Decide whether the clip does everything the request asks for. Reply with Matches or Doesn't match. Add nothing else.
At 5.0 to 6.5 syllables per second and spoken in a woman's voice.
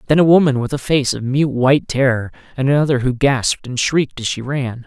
Doesn't match